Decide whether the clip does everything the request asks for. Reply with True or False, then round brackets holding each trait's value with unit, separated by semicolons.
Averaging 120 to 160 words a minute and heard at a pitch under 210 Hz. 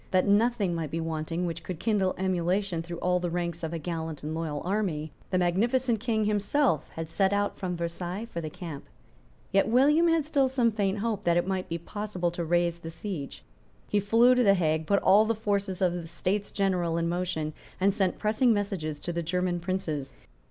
False (205 wpm; 185 Hz)